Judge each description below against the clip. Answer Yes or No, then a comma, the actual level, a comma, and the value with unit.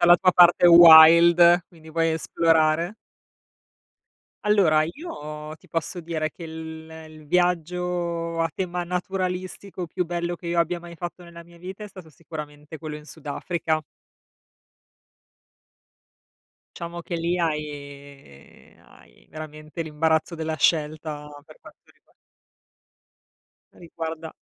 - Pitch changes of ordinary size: No, narrow, 2.0 semitones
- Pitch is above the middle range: No, medium, 165 Hz